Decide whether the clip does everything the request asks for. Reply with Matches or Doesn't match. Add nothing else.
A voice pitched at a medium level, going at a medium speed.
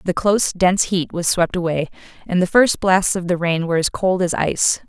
Doesn't match